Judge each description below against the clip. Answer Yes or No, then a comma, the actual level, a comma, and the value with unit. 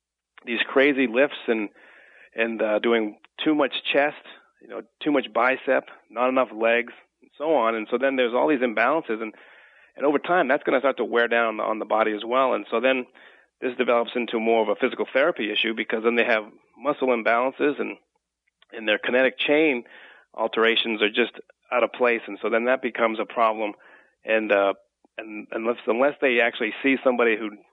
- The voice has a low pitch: Yes, low, 115 Hz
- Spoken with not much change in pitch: Yes, narrow, 2.3 semitones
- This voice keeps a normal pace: Yes, average, 195 wpm